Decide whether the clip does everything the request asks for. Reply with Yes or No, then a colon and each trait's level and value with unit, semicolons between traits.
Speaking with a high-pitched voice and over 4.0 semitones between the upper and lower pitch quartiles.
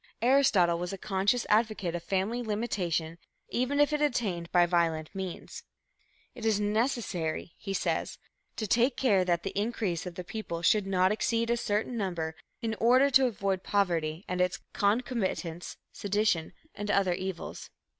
Yes: high, 200 Hz; average, 4.6 semitones